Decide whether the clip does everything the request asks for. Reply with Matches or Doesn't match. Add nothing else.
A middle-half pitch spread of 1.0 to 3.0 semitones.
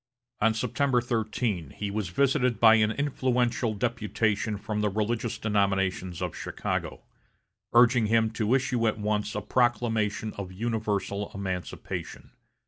Matches